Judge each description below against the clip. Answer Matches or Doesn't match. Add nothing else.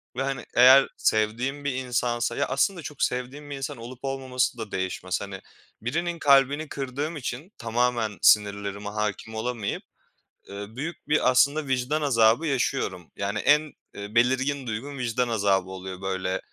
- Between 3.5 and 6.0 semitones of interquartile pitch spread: Matches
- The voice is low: Matches